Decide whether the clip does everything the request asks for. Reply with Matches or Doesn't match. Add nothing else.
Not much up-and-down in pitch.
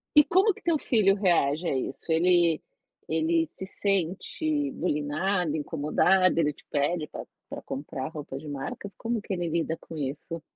Doesn't match